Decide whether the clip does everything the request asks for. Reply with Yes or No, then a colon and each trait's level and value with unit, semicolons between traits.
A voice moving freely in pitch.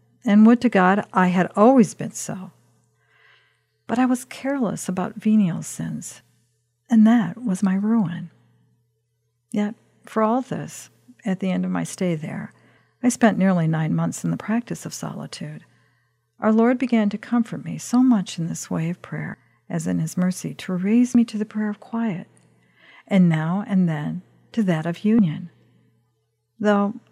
Yes: wide, 5.9 semitones